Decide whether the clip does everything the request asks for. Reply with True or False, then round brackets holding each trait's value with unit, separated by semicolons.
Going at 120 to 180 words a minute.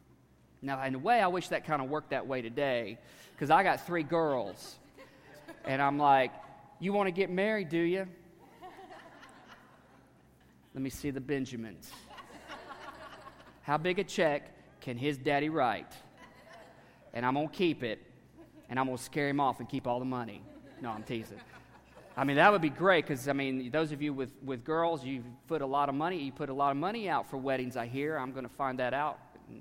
False (205 wpm)